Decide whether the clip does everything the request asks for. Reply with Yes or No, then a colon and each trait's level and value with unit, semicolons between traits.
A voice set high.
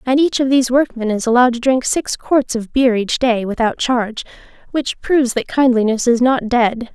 Yes: high, 245 Hz